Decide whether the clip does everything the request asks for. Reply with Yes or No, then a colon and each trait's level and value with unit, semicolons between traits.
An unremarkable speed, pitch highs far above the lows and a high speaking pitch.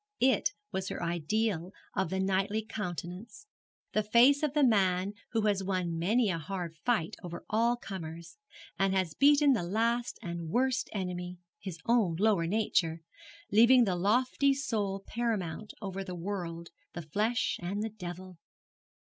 No: average, 150 wpm; average, 4.2 semitones; high, 195 Hz